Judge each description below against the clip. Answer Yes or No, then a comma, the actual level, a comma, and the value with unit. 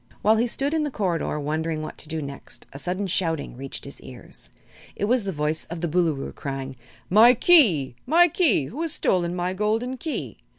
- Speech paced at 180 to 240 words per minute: Yes, average, 200 wpm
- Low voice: No, medium, 175 Hz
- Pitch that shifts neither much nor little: No, wide, 7.6 semitones